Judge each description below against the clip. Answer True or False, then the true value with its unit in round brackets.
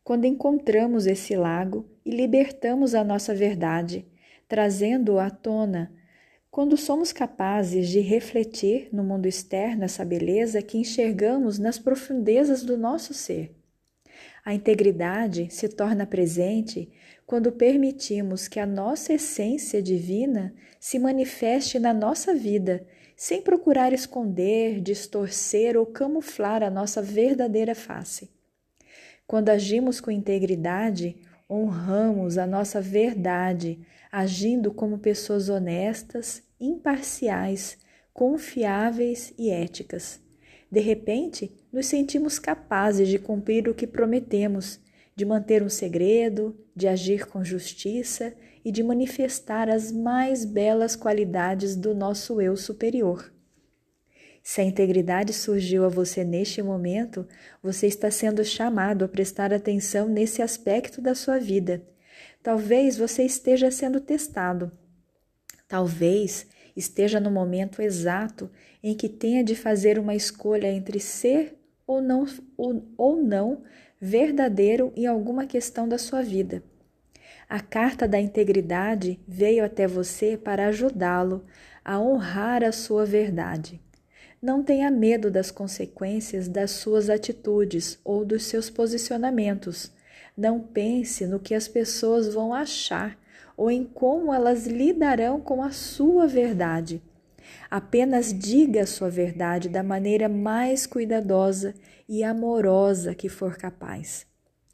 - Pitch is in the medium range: False (215 Hz)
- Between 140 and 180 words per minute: False (120 wpm)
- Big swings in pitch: False (3.6 semitones)